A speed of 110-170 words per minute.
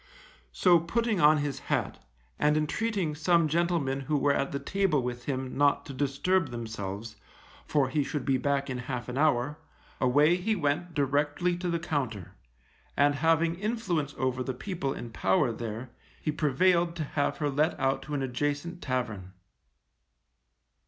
Yes: average, 160 wpm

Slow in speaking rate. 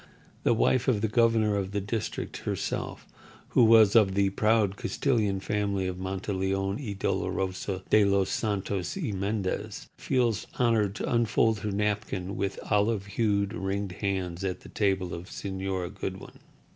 No: average, 150 wpm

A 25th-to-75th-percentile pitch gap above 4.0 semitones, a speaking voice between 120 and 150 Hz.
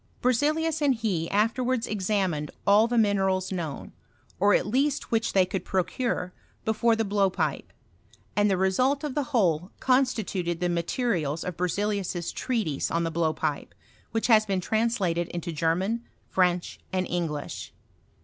No: average, 4.9 semitones; high, 195 Hz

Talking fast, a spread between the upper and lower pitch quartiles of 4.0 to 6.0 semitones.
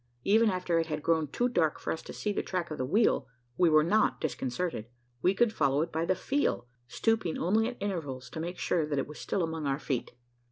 Yes: fast, 235 wpm; average, 4.7 semitones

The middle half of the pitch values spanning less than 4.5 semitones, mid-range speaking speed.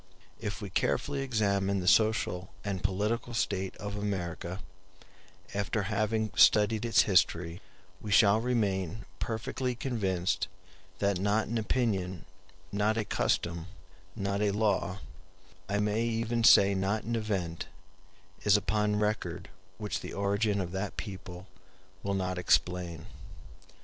No: narrow, 2.5 semitones; slow, 125 wpm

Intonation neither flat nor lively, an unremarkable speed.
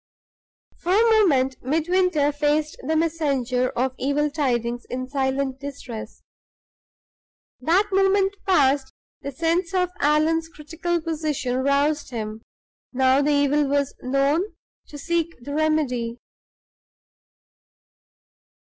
No: average, 3.8 semitones; slow, 105 wpm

